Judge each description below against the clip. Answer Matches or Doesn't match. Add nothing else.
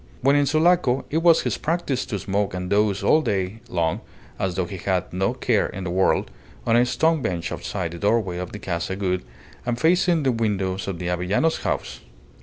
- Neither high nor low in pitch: Doesn't match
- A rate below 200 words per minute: Doesn't match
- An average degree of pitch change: Doesn't match